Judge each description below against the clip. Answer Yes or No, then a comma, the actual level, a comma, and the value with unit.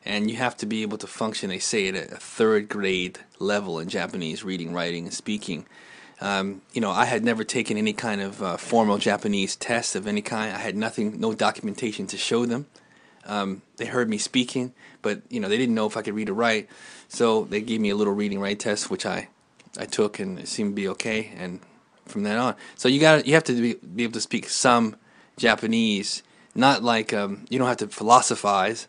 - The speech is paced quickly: Yes, fast, 220 wpm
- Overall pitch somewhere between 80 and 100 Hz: No, low, 110 Hz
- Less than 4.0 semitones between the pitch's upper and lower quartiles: Yes, average, 3.0 semitones